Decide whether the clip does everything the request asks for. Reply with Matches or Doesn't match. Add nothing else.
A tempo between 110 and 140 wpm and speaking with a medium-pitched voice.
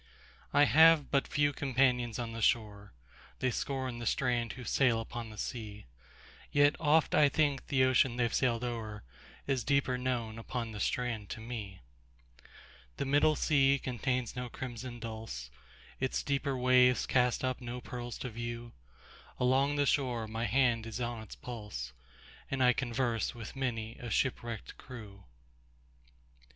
Doesn't match